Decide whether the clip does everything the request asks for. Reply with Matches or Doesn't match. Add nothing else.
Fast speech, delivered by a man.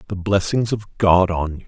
Matches